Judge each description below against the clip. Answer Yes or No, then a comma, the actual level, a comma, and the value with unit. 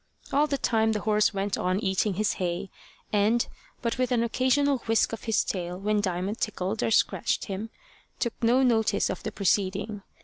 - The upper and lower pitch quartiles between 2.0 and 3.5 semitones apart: Yes, average, 3.1 semitones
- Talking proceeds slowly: No, average, 190 wpm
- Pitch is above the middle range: Yes, high, 215 Hz